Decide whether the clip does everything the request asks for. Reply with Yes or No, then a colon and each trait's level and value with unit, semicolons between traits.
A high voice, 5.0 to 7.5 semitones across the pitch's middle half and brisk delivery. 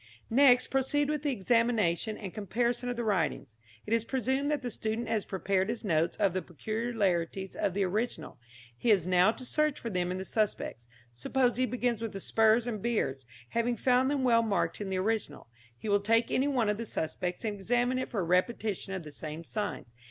No: high, 220 Hz; average, 4.5 semitones; fast, 210 wpm